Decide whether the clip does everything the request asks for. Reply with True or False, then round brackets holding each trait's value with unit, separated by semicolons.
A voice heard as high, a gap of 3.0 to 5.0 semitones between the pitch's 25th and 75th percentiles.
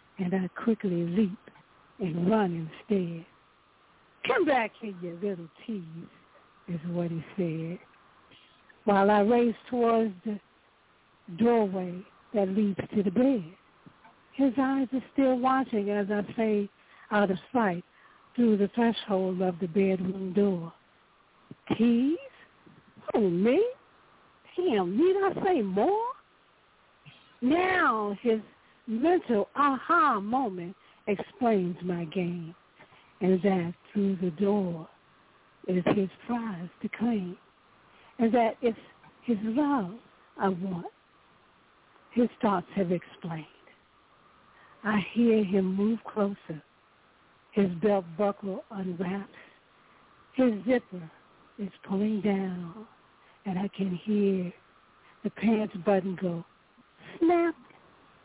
True (205 Hz; 3.9 semitones)